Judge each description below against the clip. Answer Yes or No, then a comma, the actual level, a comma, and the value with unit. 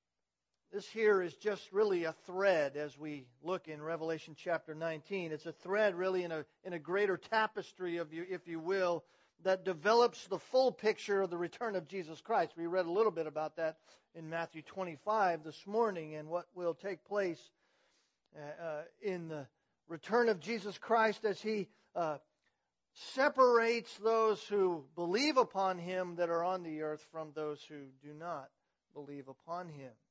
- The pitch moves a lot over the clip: No, average, 4.2 semitones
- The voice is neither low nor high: Yes, medium, 180 Hz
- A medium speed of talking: Yes, average, 165 wpm